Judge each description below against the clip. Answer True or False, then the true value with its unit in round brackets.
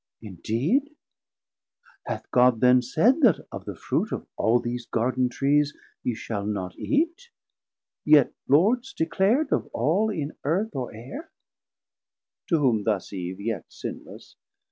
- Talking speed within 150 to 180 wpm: False (135 wpm)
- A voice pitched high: False (135 Hz)